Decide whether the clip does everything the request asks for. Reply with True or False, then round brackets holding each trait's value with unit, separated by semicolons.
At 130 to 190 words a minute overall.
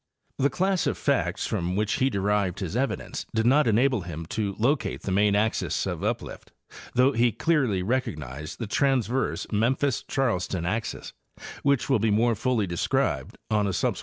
True (170 wpm)